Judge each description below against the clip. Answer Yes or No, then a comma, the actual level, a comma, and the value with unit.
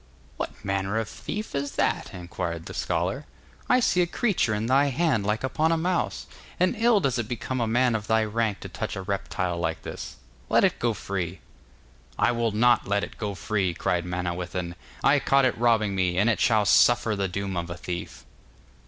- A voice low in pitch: Yes, low, 110 Hz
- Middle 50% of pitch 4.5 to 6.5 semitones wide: Yes, average, 5.2 semitones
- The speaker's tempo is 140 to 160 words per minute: No, average, 200 wpm